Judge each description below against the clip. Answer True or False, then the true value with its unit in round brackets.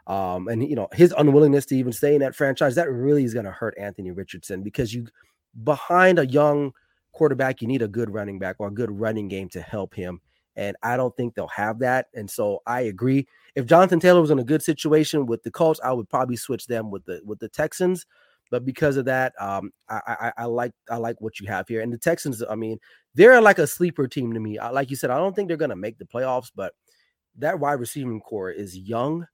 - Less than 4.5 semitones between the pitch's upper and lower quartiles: False (5.0 semitones)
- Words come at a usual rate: False (240 wpm)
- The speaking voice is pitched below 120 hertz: False (125 Hz)